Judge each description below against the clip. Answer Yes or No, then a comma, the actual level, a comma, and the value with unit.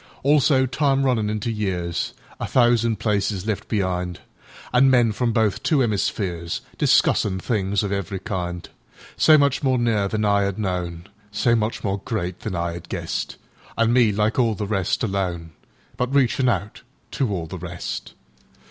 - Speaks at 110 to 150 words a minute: Yes, average, 140 wpm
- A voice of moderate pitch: No, low, 105 Hz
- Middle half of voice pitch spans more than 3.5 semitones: Yes, average, 4.1 semitones